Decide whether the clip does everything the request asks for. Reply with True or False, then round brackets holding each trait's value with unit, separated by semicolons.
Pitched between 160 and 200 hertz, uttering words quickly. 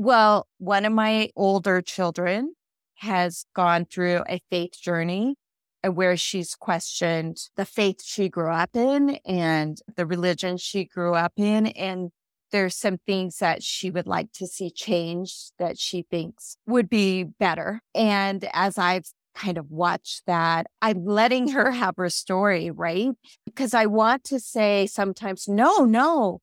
False (190 Hz; 150 wpm)